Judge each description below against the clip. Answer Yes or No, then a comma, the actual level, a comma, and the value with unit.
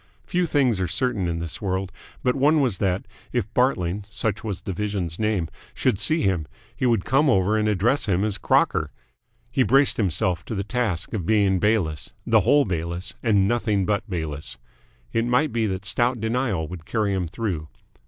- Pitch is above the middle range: No, low, 105 Hz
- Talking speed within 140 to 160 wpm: No, average, 185 wpm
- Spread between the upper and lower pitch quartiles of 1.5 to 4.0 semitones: No, average, 4.6 semitones